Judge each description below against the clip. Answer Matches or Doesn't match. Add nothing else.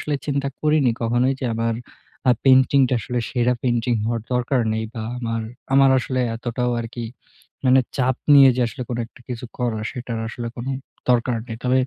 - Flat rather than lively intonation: Matches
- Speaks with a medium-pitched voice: Doesn't match